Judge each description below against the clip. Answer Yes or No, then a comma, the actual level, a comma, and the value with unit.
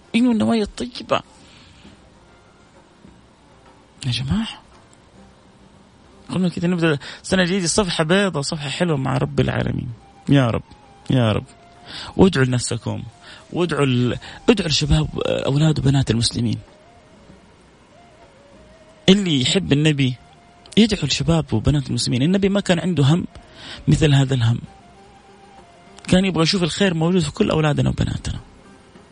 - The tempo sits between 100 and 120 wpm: Yes, average, 110 wpm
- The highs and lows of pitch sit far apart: Yes, wide, 5.8 semitones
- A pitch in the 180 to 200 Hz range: No, medium, 155 Hz